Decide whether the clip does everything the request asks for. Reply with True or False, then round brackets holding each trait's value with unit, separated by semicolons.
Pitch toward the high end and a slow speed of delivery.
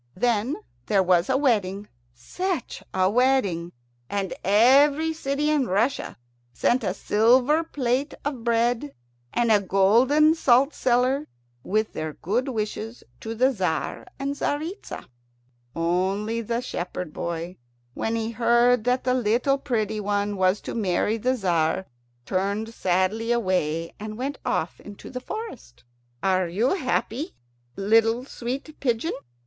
True (230 Hz; 130 wpm)